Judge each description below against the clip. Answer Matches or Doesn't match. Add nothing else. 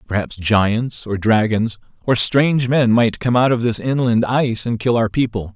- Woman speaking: Doesn't match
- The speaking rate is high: Doesn't match